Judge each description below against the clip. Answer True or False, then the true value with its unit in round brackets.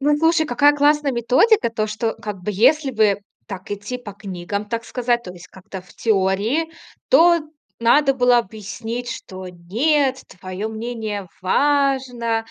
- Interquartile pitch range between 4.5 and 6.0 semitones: True (5.1 semitones)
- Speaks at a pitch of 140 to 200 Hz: False (230 Hz)